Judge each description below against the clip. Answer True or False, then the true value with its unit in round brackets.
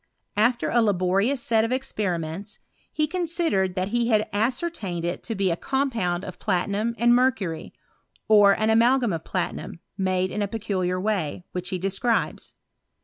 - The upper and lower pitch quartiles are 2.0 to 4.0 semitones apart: False (4.4 semitones)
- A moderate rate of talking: True (160 wpm)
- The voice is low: False (205 Hz)